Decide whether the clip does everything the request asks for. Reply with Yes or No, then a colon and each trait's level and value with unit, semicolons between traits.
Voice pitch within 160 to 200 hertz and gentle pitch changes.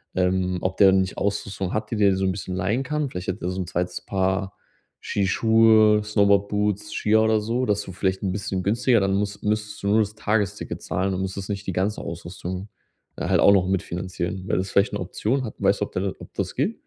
No: low, 100 Hz; narrow, 2.1 semitones